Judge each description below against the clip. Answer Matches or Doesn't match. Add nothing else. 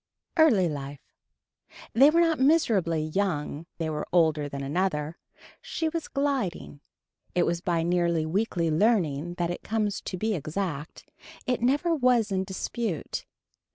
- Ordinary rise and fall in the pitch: Doesn't match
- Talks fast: Doesn't match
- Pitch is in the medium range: Matches